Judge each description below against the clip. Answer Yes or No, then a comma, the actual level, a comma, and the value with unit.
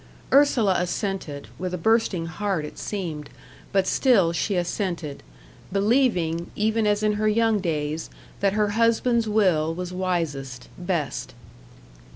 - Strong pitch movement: No, average, 4.4 semitones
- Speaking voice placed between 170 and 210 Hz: Yes, medium, 185 Hz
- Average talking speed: No, slow, 130 wpm